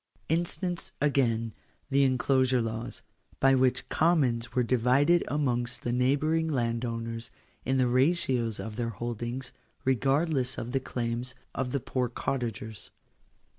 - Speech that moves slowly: Yes, slow, 130 wpm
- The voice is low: Yes, low, 125 Hz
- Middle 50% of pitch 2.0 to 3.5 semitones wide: Yes, average, 2.7 semitones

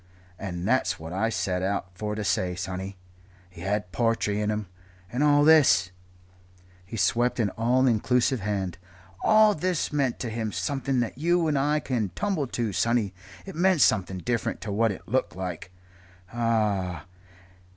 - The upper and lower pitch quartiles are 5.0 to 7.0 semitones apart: Yes, wide, 5.5 semitones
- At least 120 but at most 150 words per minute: No, average, 160 wpm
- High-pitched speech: No, low, 110 Hz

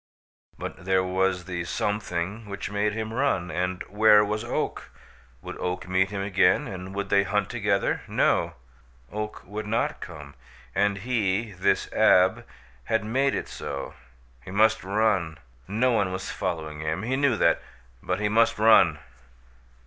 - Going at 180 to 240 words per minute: No, average, 155 wpm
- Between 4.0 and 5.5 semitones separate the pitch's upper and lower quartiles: No, average, 2.9 semitones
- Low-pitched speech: Yes, low, 100 Hz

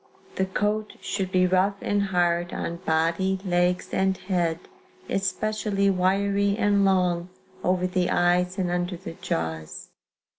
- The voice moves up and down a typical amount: No, narrow, 2.0 semitones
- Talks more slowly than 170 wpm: Yes, slow, 135 wpm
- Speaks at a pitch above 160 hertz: Yes, medium, 185 Hz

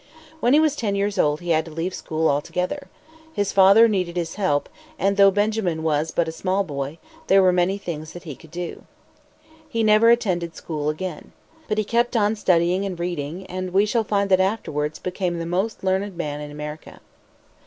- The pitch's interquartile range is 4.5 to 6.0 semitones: No, average, 4.0 semitones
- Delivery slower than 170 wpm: No, average, 200 wpm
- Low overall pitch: No, medium, 185 Hz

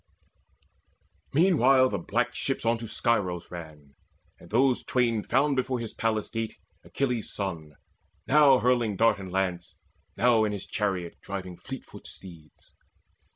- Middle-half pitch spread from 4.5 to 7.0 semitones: Yes, average, 5.2 semitones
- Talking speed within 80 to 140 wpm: Yes, slow, 135 wpm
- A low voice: Yes, low, 115 Hz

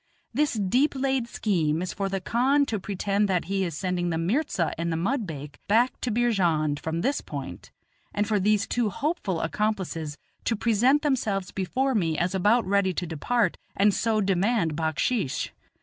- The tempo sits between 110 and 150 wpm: No, average, 170 wpm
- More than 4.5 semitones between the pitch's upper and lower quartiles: Yes, wide, 5.5 semitones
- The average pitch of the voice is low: No, high, 200 Hz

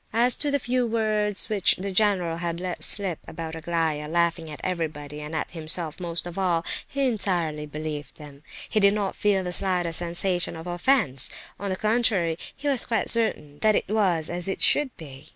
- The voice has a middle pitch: Yes, medium, 175 Hz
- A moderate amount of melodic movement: Yes, average, 4.4 semitones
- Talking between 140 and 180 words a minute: No, average, 190 wpm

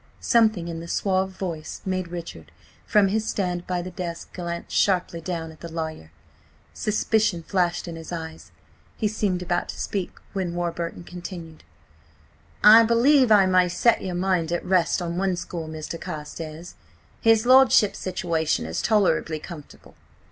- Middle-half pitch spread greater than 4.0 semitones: No, average, 2.7 semitones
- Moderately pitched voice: Yes, medium, 175 Hz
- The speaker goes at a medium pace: Yes, average, 155 wpm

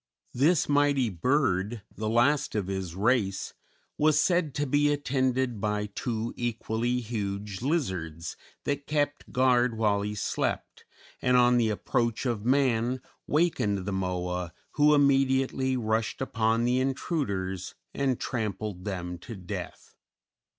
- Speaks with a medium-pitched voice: No, low, 120 Hz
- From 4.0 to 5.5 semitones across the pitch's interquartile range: Yes, average, 4.8 semitones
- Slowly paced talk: Yes, slow, 130 wpm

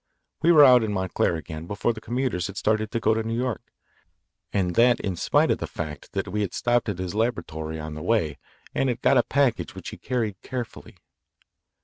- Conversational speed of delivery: No, fast, 215 wpm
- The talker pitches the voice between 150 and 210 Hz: No, low, 110 Hz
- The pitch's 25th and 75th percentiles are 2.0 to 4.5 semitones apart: No, average, 5.3 semitones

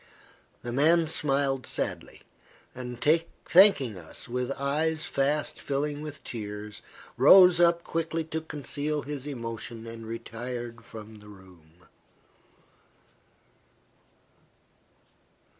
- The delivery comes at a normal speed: No, slow, 95 wpm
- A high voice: No, low, 135 Hz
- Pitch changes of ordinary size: Yes, average, 5.0 semitones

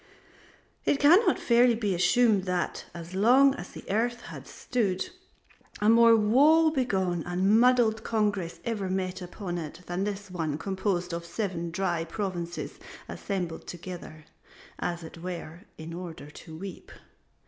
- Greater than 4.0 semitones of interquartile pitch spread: Yes, average, 4.4 semitones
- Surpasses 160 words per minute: No, average, 140 wpm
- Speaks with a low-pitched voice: No, high, 190 Hz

